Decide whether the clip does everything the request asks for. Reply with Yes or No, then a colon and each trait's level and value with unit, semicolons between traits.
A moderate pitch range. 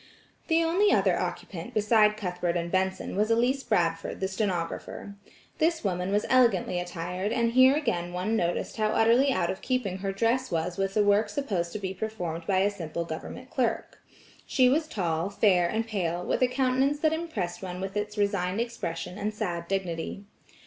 Yes: average, 4.7 semitones